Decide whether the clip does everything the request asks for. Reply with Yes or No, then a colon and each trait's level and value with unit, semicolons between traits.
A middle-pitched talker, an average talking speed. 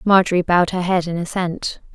Yes: medium, 180 Hz; average, 185 wpm